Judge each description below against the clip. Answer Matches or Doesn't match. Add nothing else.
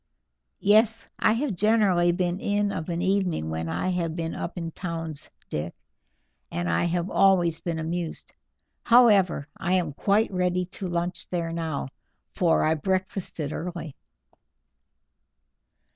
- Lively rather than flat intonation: Doesn't match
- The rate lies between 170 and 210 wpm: Doesn't match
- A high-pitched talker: Doesn't match